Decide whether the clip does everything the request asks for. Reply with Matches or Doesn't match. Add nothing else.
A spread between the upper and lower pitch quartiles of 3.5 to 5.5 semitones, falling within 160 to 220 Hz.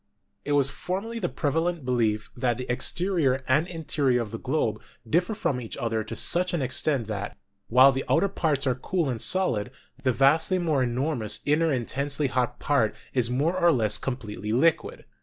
Doesn't match